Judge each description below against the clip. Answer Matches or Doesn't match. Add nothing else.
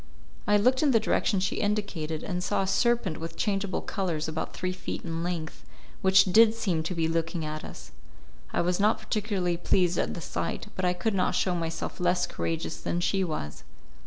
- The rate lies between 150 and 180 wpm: Doesn't match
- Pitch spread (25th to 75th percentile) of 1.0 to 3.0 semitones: Doesn't match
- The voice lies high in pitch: Doesn't match